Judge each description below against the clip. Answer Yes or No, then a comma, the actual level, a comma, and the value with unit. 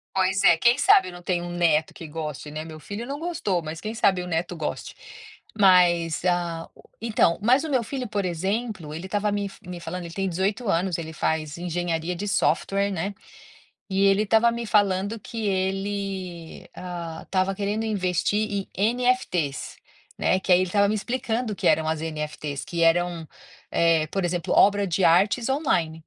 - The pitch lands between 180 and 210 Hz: Yes, medium, 185 Hz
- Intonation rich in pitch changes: No, average, 3.6 semitones